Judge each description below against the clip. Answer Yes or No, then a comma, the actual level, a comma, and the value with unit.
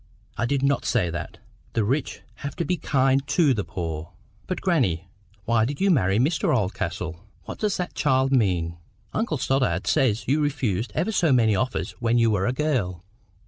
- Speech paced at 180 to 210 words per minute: Yes, average, 185 wpm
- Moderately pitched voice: No, low, 125 Hz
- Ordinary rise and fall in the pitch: No, wide, 6.8 semitones